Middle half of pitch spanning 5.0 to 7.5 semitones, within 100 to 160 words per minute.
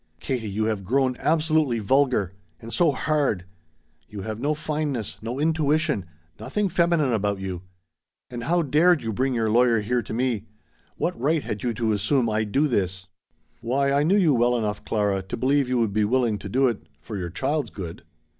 No: wide, 5.4 semitones; average, 190 wpm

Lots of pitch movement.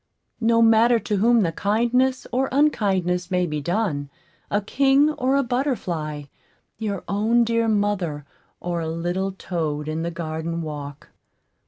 Yes: wide, 5.9 semitones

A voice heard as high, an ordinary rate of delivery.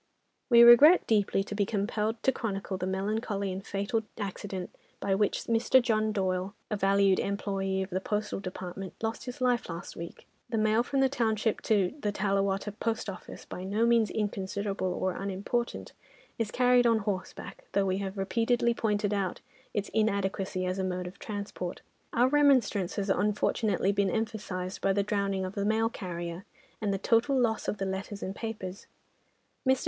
Yes: high, 200 Hz; average, 175 wpm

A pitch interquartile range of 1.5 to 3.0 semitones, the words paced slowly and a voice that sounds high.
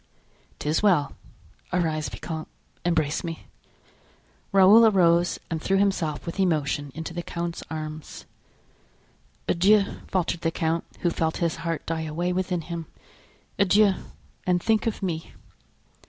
No: average, 2.7 semitones; slow, 125 wpm; medium, 170 Hz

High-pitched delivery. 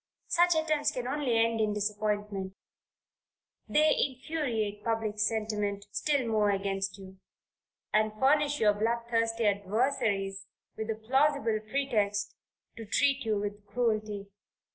Yes: high, 220 Hz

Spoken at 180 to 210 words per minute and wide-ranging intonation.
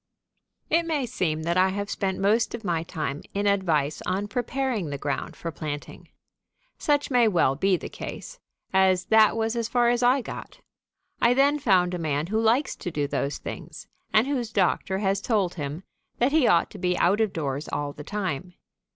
Yes: average, 195 wpm; wide, 5.9 semitones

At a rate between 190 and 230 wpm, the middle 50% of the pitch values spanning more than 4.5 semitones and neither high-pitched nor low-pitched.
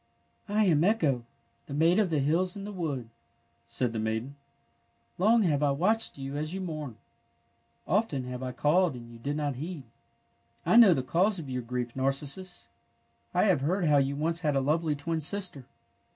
Yes: average, 195 wpm; average, 5.2 semitones; medium, 150 Hz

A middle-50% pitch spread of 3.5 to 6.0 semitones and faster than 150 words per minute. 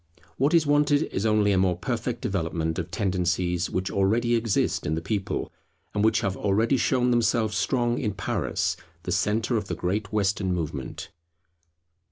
Yes: average, 4.3 semitones; average, 165 wpm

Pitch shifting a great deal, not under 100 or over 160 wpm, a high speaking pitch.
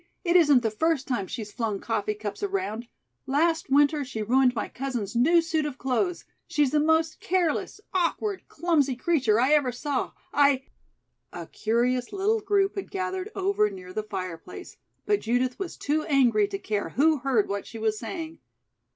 No: wide, 6.7 semitones; average, 175 wpm; very high, 275 Hz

